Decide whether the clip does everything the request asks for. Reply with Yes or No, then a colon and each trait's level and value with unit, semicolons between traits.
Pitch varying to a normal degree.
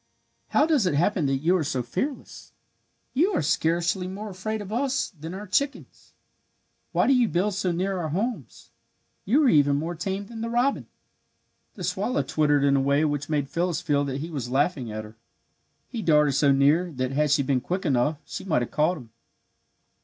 No: wide, 6.0 semitones